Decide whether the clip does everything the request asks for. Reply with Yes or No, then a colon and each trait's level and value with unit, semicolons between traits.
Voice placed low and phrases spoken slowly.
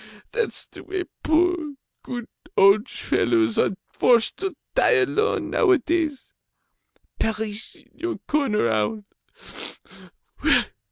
No: very high, 275 Hz; slow, 100 wpm